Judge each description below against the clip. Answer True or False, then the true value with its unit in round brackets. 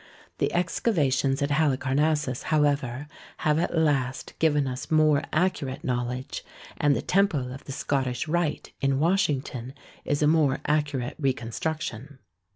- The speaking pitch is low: False (145 Hz)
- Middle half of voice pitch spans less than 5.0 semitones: True (2.8 semitones)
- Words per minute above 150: False (135 wpm)